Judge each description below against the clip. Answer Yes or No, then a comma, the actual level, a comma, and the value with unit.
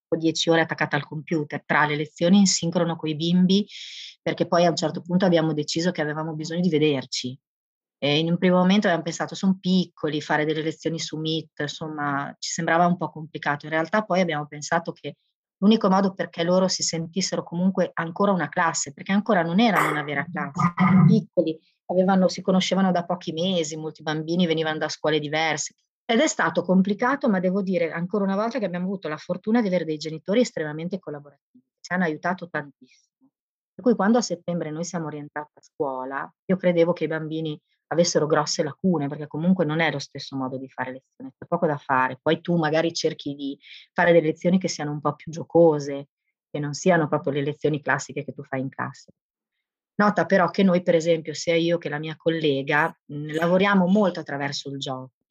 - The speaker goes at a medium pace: No, fast, 200 wpm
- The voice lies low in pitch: No, medium, 165 Hz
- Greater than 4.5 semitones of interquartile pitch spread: No, average, 3.1 semitones